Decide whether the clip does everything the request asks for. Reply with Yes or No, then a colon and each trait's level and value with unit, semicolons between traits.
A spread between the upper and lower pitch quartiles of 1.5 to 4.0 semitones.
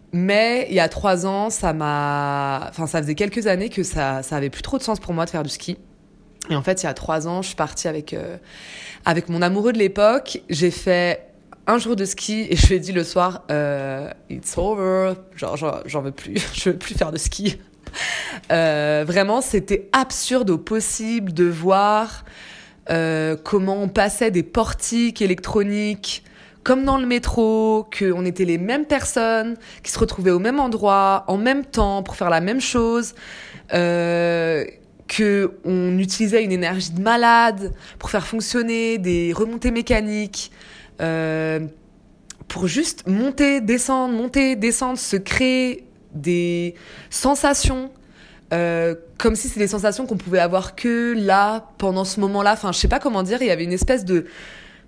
No: average, 4.7 semitones